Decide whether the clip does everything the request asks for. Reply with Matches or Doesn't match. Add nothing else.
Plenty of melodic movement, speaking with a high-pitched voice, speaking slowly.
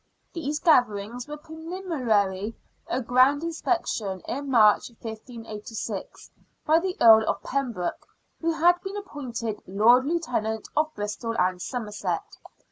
Matches